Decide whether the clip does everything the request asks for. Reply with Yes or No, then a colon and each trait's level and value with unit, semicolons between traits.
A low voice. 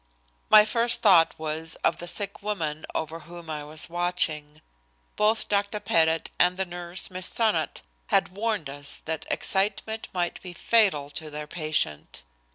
No: medium, 175 Hz